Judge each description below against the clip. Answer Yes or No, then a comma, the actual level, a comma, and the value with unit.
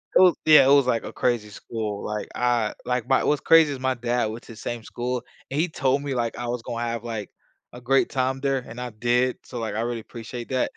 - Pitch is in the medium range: No, low, 120 Hz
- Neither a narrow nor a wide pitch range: No, narrow, 2.3 semitones